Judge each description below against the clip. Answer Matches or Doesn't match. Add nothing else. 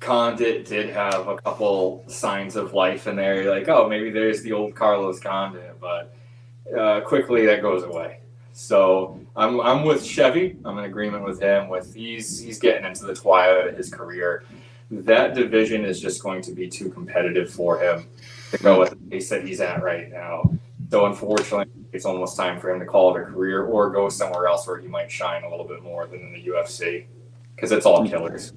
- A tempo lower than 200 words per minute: Doesn't match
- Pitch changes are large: Doesn't match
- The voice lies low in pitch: Matches